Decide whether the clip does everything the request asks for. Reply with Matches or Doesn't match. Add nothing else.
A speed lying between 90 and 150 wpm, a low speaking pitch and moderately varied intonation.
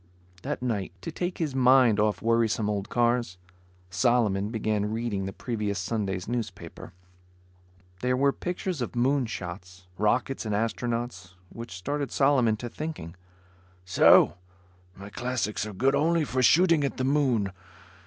Matches